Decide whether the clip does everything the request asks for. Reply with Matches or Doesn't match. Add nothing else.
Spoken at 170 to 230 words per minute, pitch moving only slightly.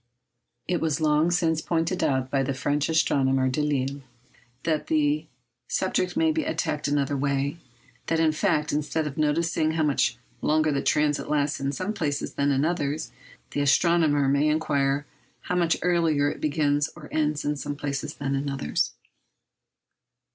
Doesn't match